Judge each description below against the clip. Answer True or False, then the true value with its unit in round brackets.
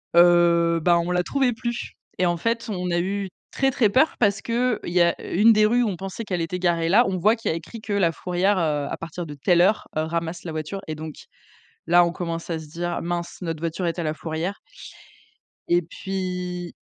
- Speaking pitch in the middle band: True (175 Hz)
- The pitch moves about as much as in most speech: True (3.1 semitones)